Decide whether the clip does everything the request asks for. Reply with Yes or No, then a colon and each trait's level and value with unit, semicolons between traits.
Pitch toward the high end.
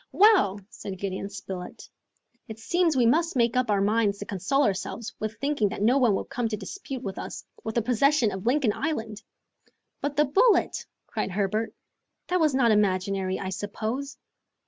Yes: high, 225 Hz